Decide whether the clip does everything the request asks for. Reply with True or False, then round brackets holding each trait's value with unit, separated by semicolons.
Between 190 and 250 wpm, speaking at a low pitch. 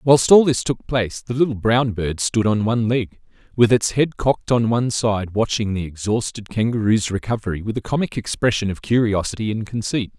True (195 wpm; 110 Hz)